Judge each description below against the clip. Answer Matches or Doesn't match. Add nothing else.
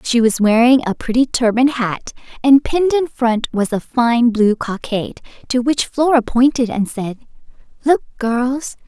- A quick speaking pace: Doesn't match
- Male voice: Doesn't match